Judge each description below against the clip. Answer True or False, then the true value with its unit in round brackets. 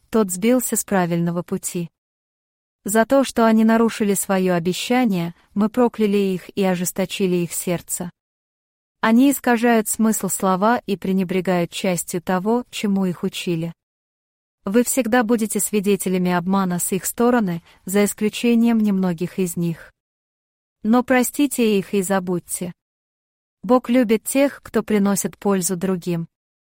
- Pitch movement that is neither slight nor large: True (3.9 semitones)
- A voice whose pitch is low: False (200 Hz)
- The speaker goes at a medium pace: False (125 wpm)